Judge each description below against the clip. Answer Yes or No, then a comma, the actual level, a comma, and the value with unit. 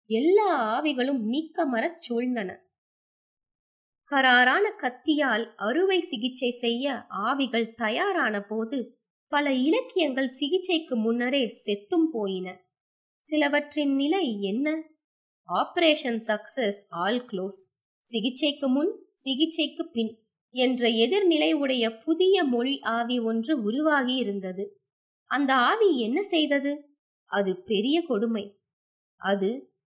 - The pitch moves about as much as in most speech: No, wide, 5.7 semitones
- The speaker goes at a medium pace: Yes, average, 90 wpm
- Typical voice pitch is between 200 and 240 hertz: No, very high, 255 Hz